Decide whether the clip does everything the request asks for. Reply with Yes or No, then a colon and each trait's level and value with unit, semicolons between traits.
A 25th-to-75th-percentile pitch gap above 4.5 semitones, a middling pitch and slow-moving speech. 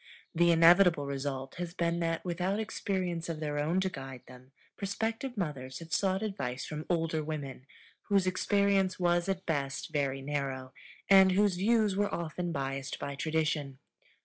No: average, 5.1 semitones; medium, 165 Hz; average, 155 wpm